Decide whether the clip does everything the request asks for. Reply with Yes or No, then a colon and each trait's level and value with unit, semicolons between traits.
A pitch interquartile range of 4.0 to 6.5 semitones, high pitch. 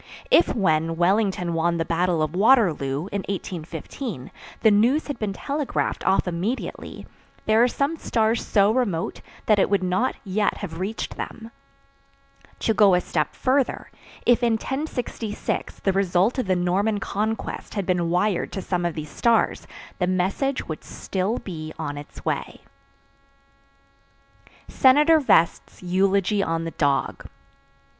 Yes: average, 4.6 semitones; high, 195 Hz